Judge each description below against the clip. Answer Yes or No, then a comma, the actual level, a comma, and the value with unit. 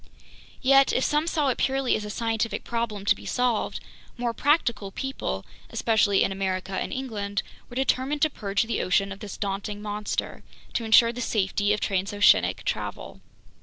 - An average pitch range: Yes, average, 4.1 semitones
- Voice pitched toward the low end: No, high, 220 Hz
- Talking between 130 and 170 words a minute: Yes, average, 165 wpm